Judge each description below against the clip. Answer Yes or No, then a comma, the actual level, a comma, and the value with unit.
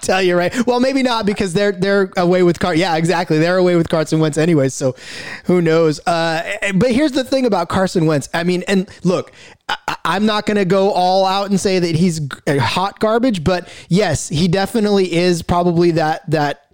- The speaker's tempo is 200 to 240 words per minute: Yes, fast, 205 wpm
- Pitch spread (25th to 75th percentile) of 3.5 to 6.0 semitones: No, average, 3.1 semitones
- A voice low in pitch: No, medium, 180 Hz